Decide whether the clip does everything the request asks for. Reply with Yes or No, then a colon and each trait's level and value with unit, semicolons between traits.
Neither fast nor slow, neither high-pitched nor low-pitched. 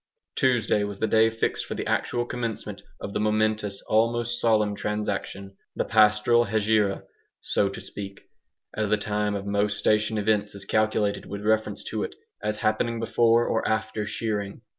No: average, 160 wpm; low, 105 Hz